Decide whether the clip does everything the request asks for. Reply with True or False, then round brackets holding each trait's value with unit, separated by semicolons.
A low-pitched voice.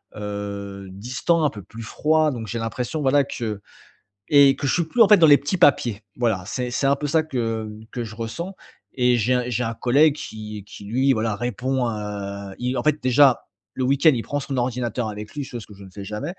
True (125 Hz)